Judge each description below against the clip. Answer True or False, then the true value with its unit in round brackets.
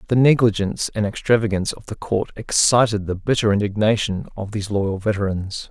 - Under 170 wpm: True (160 wpm)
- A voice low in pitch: True (105 Hz)